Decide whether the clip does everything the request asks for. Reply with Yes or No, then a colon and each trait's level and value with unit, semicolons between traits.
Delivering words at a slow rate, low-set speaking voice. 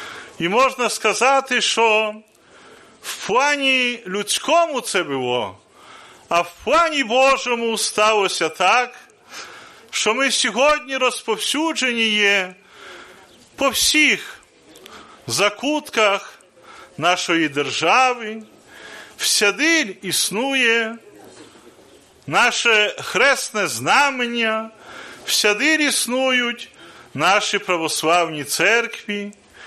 No: slow, 70 wpm; high, 230 Hz